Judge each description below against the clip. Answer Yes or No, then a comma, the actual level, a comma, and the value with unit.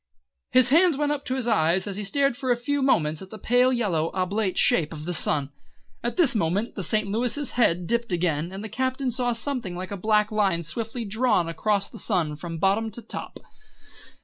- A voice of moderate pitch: No, high, 215 Hz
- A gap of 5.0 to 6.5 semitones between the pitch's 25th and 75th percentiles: Yes, wide, 5.5 semitones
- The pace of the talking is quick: Yes, fast, 210 wpm